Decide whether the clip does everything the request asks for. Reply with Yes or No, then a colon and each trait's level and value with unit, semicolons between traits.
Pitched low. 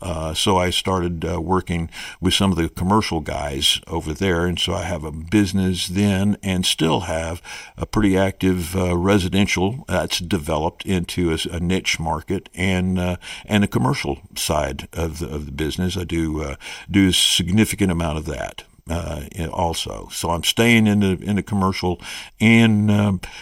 Yes: very low, 90 Hz